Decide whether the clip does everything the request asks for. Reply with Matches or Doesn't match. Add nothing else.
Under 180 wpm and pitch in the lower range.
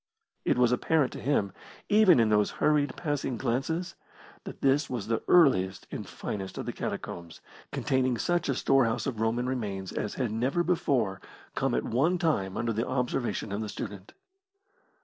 Matches